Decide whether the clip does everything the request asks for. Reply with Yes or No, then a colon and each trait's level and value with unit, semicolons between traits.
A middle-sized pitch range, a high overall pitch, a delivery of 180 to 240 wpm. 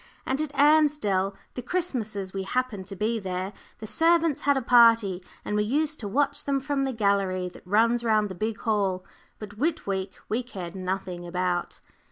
No: wide, 5.7 semitones; high, 215 Hz; average, 185 wpm